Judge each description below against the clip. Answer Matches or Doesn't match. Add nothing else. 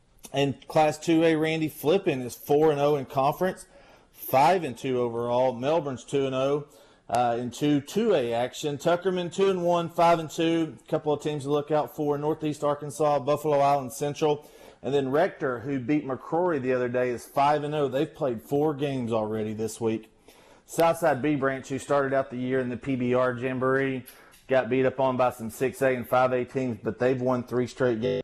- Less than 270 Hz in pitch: Matches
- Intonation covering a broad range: Doesn't match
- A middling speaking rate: Matches